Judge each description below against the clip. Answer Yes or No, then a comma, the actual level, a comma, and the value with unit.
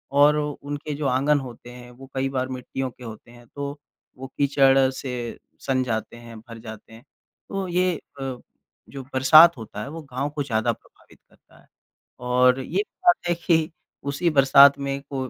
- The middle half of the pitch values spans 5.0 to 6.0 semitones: No, narrow, 2.6 semitones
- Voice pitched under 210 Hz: Yes, low, 135 Hz